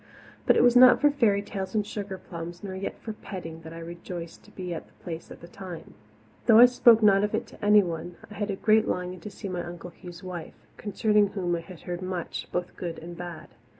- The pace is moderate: No, fast, 230 wpm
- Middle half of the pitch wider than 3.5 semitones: No, average, 3.2 semitones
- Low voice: No, medium, 185 Hz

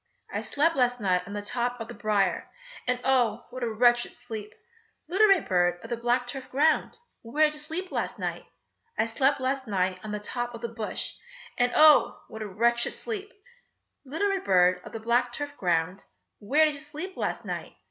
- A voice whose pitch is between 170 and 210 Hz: No, high, 245 Hz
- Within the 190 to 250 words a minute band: Yes, average, 200 wpm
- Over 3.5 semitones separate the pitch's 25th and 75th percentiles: Yes, wide, 5.5 semitones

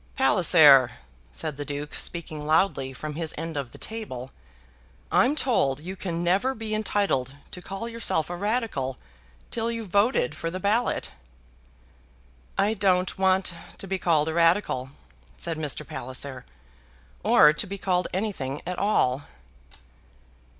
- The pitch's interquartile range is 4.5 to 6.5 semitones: Yes, wide, 5.5 semitones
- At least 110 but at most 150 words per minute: Yes, average, 140 wpm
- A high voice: No, medium, 175 Hz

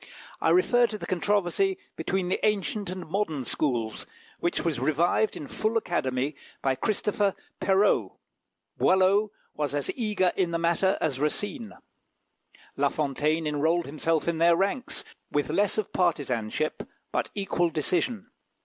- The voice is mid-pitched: Yes, medium, 175 Hz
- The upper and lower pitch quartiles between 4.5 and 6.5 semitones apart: Yes, average, 5.3 semitones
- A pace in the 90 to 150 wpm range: Yes, average, 140 wpm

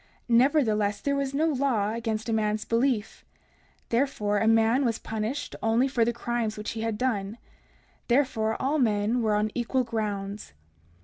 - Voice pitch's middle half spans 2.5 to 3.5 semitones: Yes, average, 3.0 semitones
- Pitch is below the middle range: No, high, 225 Hz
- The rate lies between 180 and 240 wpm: No, average, 160 wpm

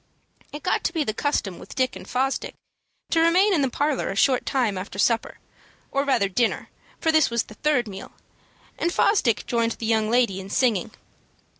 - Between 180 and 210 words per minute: Yes, average, 190 wpm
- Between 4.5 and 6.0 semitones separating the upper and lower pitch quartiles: Yes, wide, 5.4 semitones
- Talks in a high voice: Yes, very high, 250 Hz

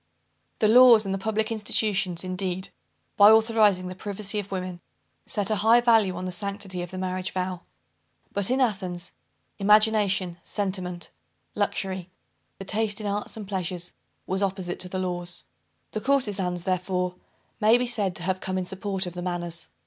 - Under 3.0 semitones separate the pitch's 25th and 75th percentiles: Yes, narrow, 2.5 semitones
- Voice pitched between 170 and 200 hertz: Yes, high, 190 Hz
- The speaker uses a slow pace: No, average, 165 wpm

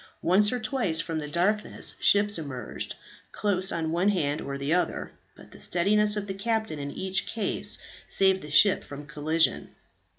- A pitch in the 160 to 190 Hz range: Yes, medium, 185 Hz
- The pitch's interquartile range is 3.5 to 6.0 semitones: Yes, average, 5.1 semitones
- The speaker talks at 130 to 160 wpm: No, average, 170 wpm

